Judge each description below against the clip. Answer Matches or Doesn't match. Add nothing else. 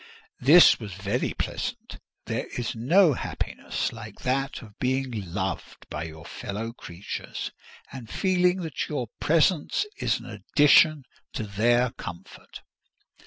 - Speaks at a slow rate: Matches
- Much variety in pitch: Matches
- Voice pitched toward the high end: Doesn't match